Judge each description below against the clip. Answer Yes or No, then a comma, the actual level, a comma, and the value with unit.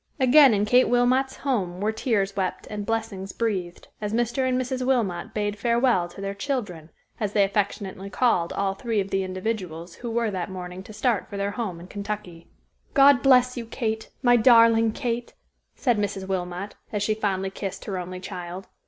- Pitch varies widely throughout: No, average, 3.8 semitones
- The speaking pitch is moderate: No, high, 210 Hz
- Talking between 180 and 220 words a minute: Yes, average, 185 wpm